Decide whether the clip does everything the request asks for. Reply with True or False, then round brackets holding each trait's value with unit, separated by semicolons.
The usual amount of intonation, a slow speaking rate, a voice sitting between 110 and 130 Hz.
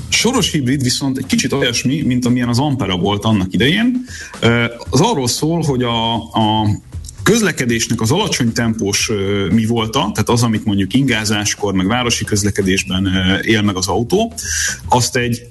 False (4.1 semitones; 150 wpm; 115 Hz)